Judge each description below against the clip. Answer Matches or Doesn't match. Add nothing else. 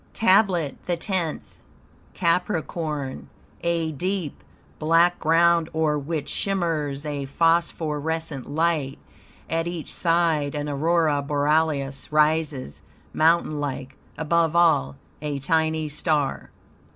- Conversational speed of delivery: Doesn't match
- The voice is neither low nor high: Matches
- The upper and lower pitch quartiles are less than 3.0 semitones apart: Matches